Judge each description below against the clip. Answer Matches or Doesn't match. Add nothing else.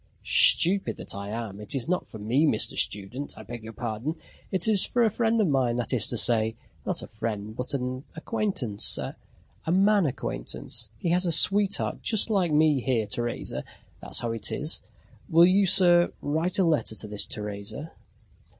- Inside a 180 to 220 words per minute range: Matches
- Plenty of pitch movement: Matches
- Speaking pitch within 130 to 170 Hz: Matches